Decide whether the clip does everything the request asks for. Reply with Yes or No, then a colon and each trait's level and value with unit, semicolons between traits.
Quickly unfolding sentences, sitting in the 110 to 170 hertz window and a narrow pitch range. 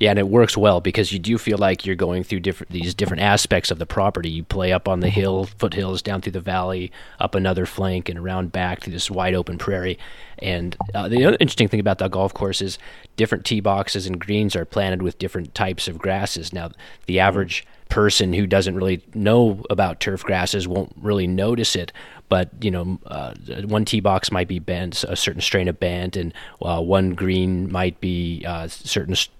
No: fast, 210 wpm; very low, 95 Hz; narrow, 2.0 semitones